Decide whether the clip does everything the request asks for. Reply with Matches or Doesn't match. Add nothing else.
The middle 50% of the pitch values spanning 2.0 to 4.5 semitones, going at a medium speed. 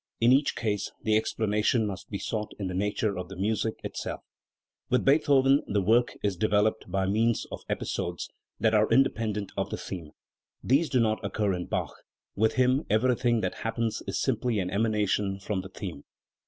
Matches